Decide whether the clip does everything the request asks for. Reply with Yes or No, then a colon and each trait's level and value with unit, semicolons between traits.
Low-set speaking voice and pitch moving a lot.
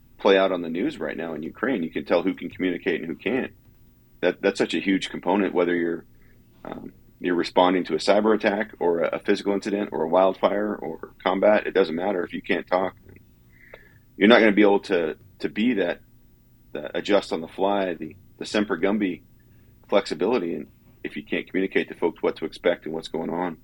No: very low, 95 Hz; average, 2.9 semitones